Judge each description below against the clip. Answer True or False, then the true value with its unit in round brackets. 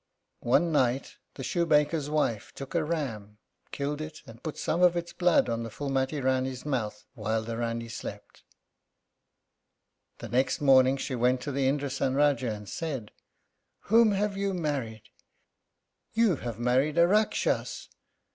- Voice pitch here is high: False (135 Hz)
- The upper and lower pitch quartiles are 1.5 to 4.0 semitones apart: False (4.8 semitones)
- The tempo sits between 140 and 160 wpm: True (145 wpm)